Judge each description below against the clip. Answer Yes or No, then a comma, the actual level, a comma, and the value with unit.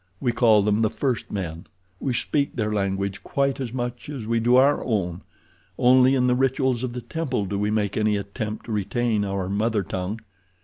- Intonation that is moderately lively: Yes, average, 3.9 semitones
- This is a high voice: No, low, 110 Hz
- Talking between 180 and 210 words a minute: Yes, average, 190 wpm